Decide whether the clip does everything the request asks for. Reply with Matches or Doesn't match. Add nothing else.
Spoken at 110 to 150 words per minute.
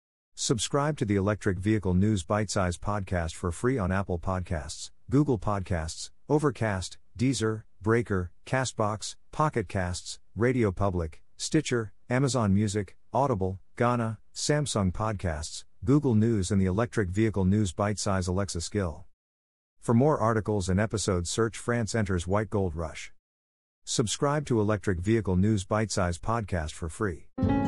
Matches